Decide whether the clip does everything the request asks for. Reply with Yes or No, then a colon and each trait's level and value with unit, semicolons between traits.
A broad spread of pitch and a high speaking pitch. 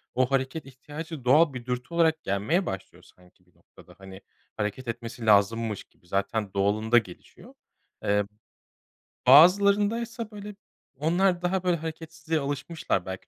No: wide, 8.2 semitones; low, 130 Hz